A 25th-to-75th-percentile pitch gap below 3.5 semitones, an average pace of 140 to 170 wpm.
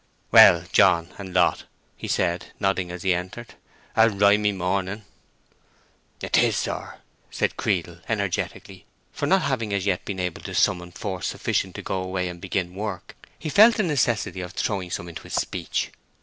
Yes: average, 2.8 semitones; average, 165 wpm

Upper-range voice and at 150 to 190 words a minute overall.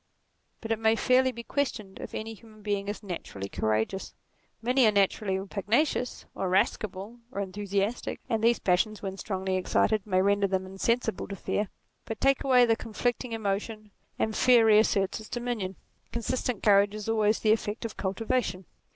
Yes: high, 215 Hz; average, 170 wpm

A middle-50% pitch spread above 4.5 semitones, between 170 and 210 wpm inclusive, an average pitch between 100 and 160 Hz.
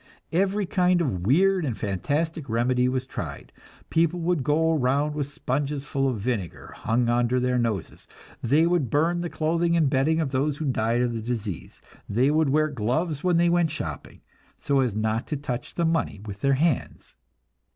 Yes: average, 5.0 semitones; average, 185 wpm; medium, 140 Hz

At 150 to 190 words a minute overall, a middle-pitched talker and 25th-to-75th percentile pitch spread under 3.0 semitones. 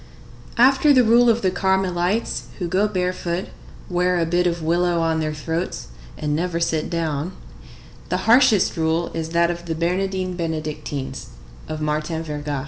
Yes: average, 155 wpm; medium, 175 Hz; narrow, 2.6 semitones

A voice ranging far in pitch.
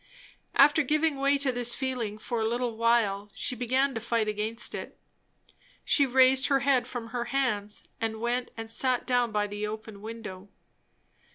No: average, 3.1 semitones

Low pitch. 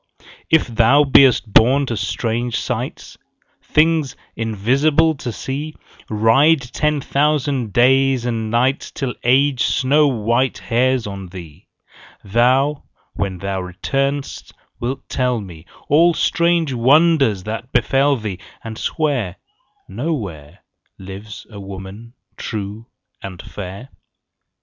Yes: low, 120 Hz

